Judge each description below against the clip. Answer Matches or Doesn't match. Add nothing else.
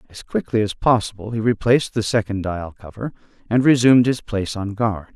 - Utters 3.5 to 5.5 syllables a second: Doesn't match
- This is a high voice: Doesn't match